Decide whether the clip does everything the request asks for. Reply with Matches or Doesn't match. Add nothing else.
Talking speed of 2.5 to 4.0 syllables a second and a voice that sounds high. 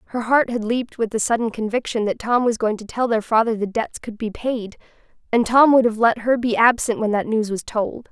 Doesn't match